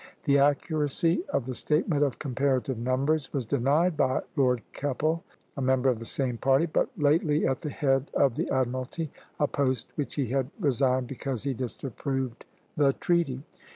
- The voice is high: No, low, 135 Hz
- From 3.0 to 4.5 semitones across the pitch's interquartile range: No, narrow, 2.4 semitones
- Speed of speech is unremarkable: Yes, average, 170 wpm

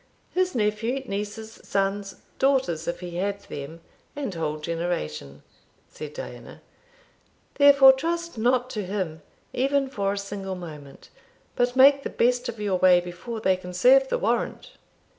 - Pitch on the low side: No, high, 205 Hz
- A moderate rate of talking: Yes, average, 145 wpm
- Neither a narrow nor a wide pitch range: No, wide, 6.5 semitones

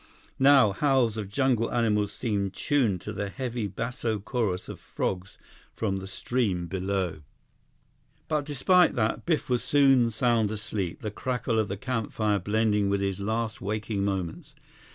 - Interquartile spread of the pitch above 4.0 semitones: No, average, 3.7 semitones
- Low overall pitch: Yes, low, 110 Hz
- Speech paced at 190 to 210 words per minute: No, average, 150 wpm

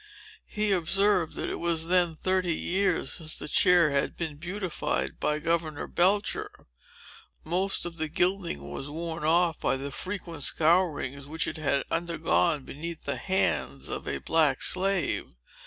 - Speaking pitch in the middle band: Yes, medium, 165 Hz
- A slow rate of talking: No, average, 150 wpm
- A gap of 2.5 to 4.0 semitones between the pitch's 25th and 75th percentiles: Yes, average, 3.2 semitones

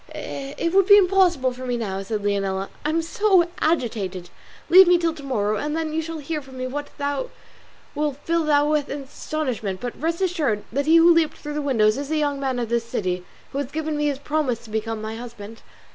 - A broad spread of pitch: Yes, wide, 5.7 semitones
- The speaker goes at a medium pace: No, fast, 220 wpm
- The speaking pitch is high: Yes, very high, 280 Hz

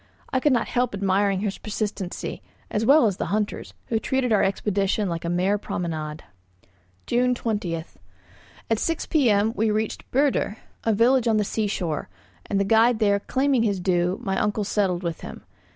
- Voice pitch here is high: Yes, high, 205 Hz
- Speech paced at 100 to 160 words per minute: No, average, 175 wpm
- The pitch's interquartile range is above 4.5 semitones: No, average, 3.5 semitones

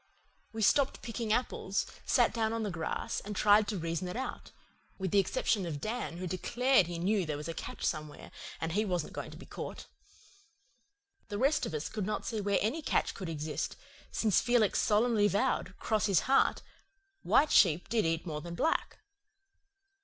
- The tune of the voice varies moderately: Yes, average, 5.0 semitones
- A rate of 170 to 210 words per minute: Yes, average, 190 wpm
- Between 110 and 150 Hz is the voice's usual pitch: No, high, 205 Hz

